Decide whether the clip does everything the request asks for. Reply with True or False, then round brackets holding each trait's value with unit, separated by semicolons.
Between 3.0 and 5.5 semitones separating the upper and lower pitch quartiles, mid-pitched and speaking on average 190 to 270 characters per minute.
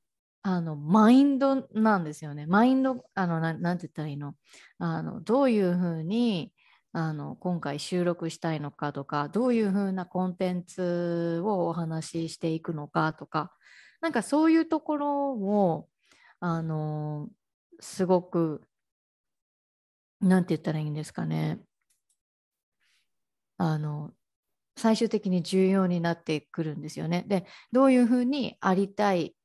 True (5.2 semitones; 175 Hz; 245 characters per minute)